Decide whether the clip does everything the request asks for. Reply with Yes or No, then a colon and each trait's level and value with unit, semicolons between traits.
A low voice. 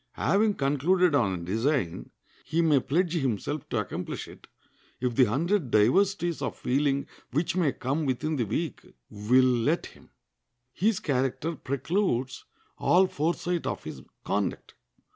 No: medium, 145 Hz